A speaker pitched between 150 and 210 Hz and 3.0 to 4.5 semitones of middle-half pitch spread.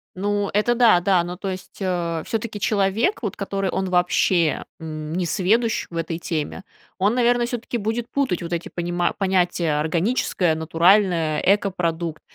Yes: medium, 185 Hz; average, 3.5 semitones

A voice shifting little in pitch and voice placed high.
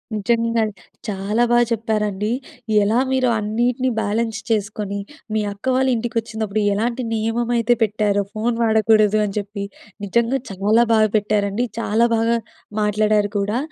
Yes: narrow, 2.0 semitones; high, 220 Hz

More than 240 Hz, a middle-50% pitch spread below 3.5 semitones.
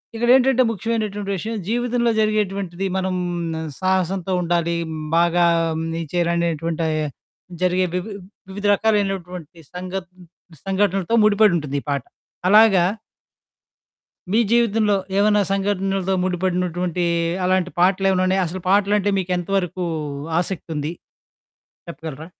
No: medium, 185 Hz; average, 2.8 semitones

